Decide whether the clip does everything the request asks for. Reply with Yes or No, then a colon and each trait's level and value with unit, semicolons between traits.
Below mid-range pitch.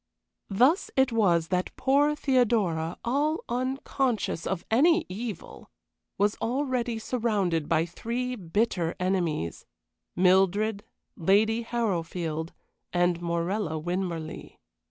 No: high, 205 Hz